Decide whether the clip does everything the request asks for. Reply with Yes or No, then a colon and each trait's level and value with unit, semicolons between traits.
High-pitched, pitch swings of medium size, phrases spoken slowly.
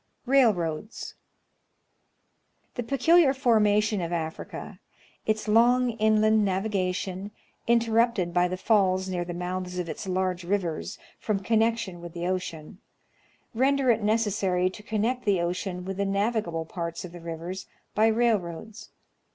Yes: high, 200 Hz; average, 3.9 semitones; slow, 130 wpm